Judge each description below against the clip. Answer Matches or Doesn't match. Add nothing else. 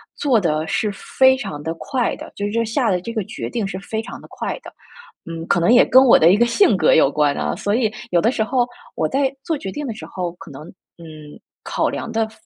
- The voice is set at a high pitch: Matches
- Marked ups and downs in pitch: Matches